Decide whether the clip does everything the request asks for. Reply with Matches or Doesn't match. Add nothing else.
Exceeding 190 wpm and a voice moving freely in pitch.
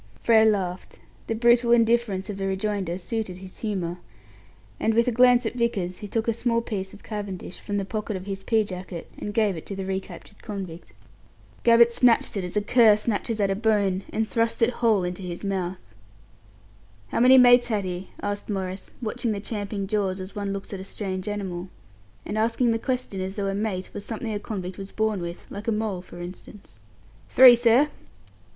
Doesn't match